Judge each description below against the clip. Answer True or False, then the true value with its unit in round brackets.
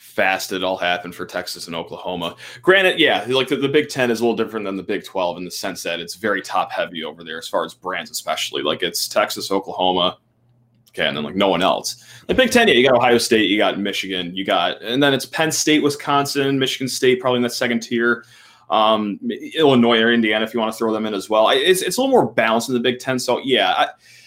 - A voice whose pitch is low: True (120 Hz)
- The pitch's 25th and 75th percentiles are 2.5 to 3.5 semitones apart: False (4.7 semitones)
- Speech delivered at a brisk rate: True (250 wpm)